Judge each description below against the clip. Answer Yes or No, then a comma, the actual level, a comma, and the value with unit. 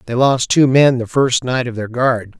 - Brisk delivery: Yes, fast, 250 wpm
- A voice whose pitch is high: No, low, 125 Hz